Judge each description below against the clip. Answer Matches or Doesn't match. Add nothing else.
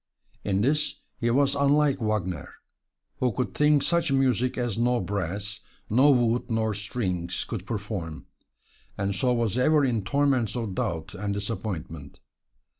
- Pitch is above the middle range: Doesn't match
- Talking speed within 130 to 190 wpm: Matches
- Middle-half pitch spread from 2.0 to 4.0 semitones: Doesn't match